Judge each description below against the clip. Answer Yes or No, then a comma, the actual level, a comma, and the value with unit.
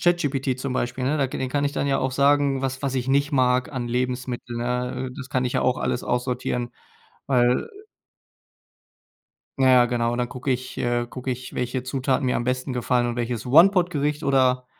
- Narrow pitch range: Yes, narrow, 1.7 semitones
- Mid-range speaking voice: No, low, 130 Hz